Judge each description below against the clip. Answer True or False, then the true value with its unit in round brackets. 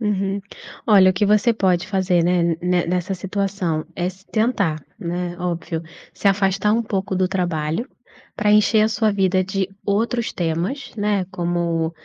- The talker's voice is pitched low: False (190 Hz)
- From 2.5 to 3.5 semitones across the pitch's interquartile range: True (2.8 semitones)